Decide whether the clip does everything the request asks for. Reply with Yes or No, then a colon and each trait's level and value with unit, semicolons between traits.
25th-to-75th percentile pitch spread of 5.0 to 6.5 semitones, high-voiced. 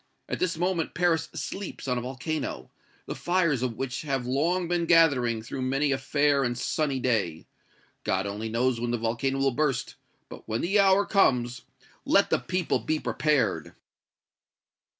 No: average, 5.3 semitones; low, 135 Hz